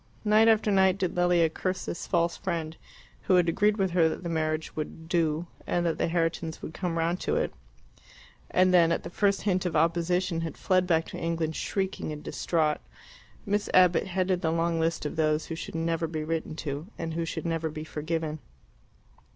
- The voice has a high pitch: No, medium, 165 Hz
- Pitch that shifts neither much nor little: No, narrow, 2.1 semitones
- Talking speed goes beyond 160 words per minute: Yes, average, 200 wpm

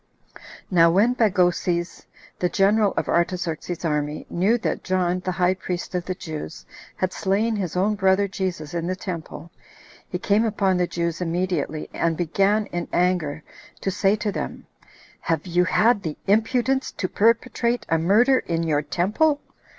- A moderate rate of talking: Yes, average, 160 wpm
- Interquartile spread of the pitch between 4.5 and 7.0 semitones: No, average, 3.3 semitones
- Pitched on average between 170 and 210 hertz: Yes, medium, 185 Hz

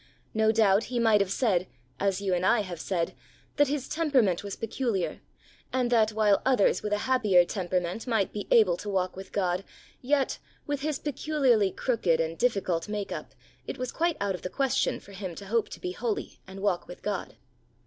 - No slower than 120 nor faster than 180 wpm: No, average, 200 wpm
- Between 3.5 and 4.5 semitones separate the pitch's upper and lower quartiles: No, average, 4.9 semitones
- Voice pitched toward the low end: No, high, 210 Hz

